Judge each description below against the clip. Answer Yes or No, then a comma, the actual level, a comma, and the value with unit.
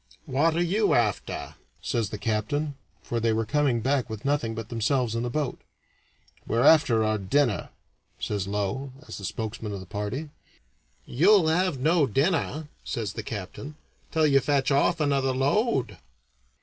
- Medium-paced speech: Yes, average, 155 wpm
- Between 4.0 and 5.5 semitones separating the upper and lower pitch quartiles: Yes, average, 5.1 semitones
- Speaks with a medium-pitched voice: No, low, 130 Hz